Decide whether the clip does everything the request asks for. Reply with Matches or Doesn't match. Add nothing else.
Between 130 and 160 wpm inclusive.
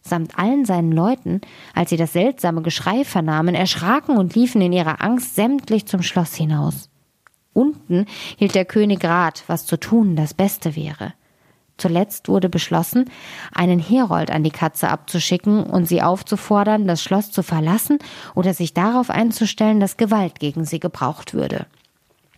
Matches